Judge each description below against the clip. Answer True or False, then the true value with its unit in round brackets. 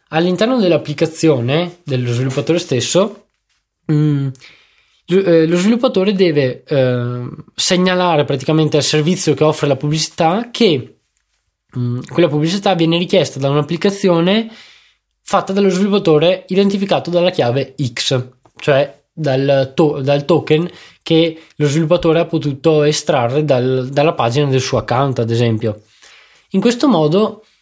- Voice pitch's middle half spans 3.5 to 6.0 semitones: True (4.6 semitones)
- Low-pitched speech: False (155 Hz)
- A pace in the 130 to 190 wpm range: False (115 wpm)